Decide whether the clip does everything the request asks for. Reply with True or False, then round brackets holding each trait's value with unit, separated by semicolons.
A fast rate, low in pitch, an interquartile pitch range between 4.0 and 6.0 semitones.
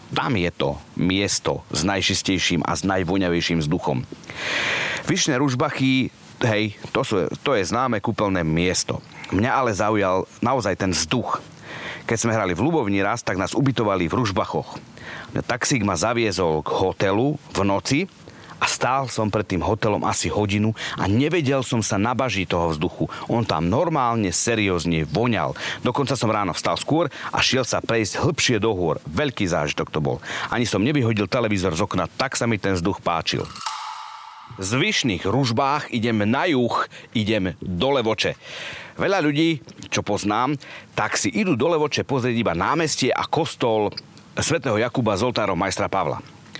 False (155 wpm; 105 Hz; 5.1 semitones)